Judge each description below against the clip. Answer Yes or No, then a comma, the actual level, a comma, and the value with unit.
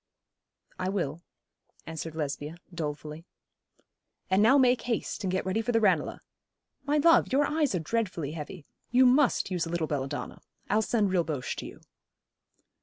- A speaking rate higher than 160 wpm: No, average, 155 wpm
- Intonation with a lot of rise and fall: Yes, wide, 6.6 semitones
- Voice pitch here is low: No, medium, 185 Hz